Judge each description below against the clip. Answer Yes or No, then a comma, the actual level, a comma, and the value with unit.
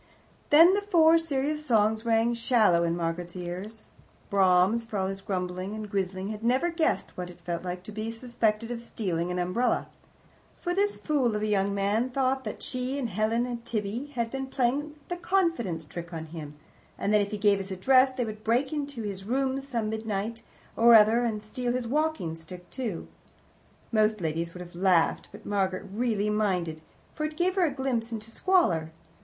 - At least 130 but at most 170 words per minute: No, average, 190 wpm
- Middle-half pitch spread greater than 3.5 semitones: Yes, wide, 5.4 semitones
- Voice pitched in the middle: No, high, 220 Hz